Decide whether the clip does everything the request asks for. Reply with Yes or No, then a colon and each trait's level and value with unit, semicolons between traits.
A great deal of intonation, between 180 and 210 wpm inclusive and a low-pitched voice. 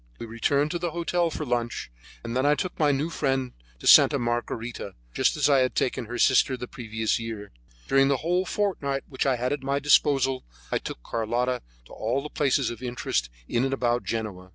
No: average, 3.4 semitones; fast, 205 wpm; low, 130 Hz